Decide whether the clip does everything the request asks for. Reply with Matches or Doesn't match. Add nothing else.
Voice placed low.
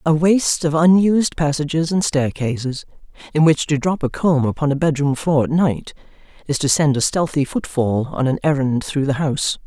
Doesn't match